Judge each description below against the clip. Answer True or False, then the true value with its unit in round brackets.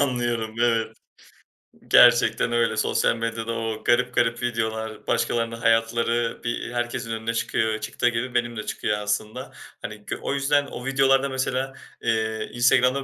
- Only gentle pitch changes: True (1.7 semitones)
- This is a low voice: True (115 Hz)